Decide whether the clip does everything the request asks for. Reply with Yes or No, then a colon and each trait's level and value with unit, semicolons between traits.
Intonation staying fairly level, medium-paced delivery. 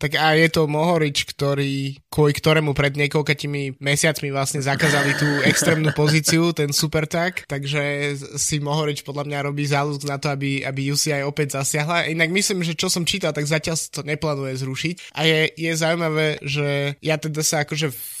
No: narrow, 1.9 semitones; fast, 180 wpm